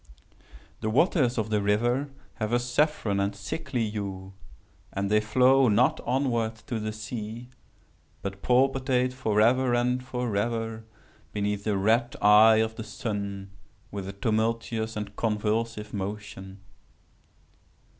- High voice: No, low, 110 Hz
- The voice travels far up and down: No, average, 3.0 semitones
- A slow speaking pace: Yes, slow, 125 wpm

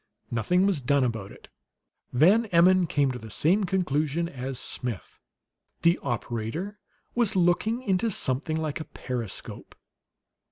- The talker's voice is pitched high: No, medium, 155 Hz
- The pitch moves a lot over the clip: Yes, wide, 6.8 semitones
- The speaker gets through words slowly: Yes, slow, 130 wpm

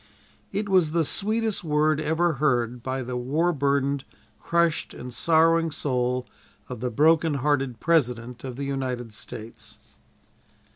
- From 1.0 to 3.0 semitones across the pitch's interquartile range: No, average, 4.6 semitones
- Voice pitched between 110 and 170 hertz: Yes, medium, 140 Hz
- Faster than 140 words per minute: No, slow, 135 wpm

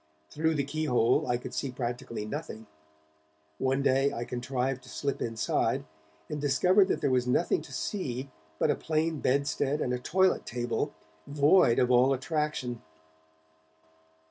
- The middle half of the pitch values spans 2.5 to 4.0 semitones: Yes, average, 3.5 semitones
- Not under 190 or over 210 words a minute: No, average, 150 wpm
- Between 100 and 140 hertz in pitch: Yes, low, 135 Hz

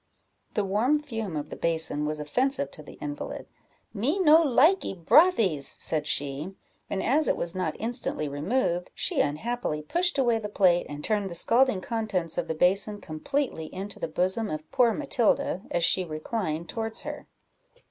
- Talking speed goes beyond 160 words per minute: Yes, average, 170 wpm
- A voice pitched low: No, high, 195 Hz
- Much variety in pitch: Yes, wide, 7.3 semitones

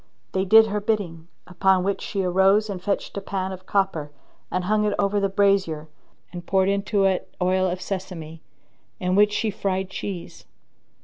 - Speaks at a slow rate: No, average, 175 wpm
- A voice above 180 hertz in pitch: Yes, high, 190 Hz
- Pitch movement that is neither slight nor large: No, narrow, 1.7 semitones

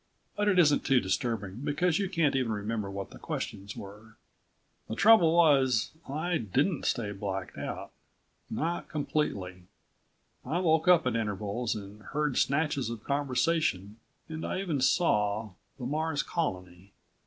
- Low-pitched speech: Yes, low, 130 Hz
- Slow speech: No, average, 145 wpm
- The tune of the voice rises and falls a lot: Yes, wide, 7.4 semitones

